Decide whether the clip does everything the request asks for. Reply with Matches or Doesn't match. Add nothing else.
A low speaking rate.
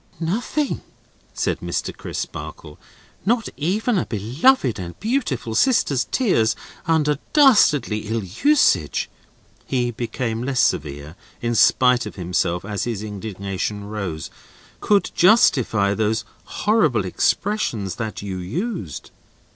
Matches